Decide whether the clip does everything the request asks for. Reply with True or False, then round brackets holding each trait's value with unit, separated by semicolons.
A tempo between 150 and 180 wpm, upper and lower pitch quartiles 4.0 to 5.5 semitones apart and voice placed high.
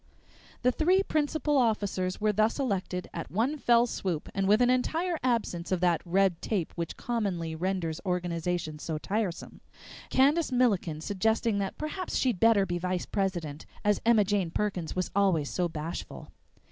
True (160 wpm; 5.2 semitones; 195 Hz)